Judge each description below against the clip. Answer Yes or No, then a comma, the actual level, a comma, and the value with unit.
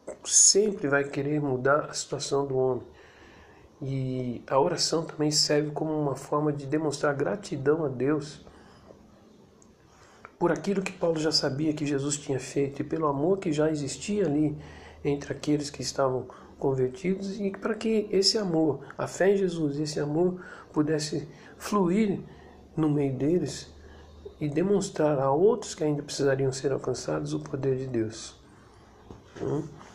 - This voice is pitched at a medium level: Yes, medium, 150 Hz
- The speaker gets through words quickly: No, average, 145 wpm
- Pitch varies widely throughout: No, average, 3.2 semitones